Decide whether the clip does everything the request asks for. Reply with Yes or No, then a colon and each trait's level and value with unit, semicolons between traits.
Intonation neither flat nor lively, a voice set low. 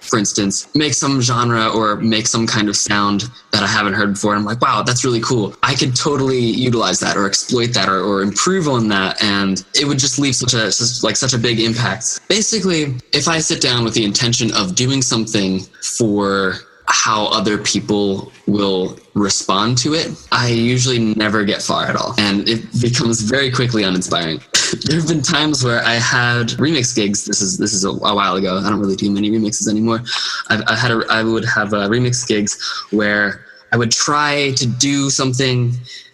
Yes: average, 3.6 semitones; low, 115 Hz